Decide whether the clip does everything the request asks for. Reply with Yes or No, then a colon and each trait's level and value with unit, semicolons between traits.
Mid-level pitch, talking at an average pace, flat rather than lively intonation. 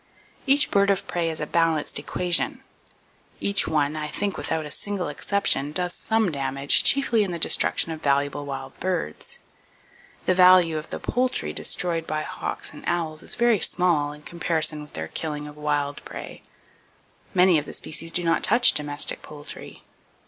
No: medium, 160 Hz; average, 170 wpm; average, 3.7 semitones